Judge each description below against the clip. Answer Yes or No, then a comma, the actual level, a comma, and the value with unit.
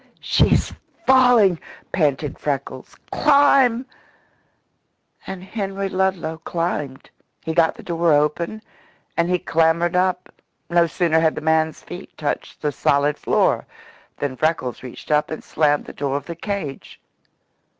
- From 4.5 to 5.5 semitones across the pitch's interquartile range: No, average, 4.0 semitones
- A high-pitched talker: No, medium, 165 Hz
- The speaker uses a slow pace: Yes, slow, 130 wpm